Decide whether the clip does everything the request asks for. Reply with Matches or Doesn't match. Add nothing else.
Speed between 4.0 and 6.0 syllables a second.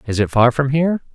Doesn't match